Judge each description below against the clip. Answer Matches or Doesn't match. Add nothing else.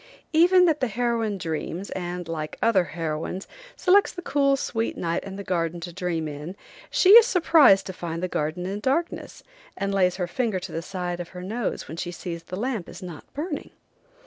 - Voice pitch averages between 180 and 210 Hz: Matches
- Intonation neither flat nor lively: Doesn't match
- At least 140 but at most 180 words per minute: Doesn't match